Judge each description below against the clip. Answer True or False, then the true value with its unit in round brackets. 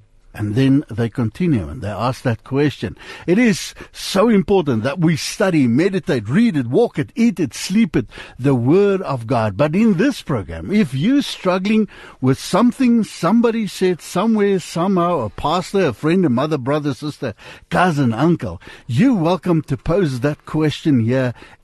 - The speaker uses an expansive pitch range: True (7.0 semitones)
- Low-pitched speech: False (155 Hz)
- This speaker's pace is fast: False (165 wpm)